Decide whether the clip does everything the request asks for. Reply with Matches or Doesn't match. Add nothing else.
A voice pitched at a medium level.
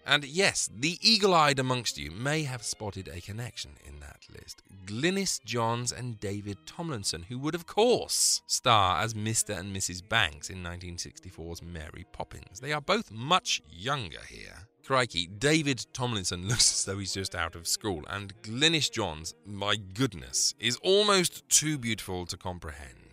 Doesn't match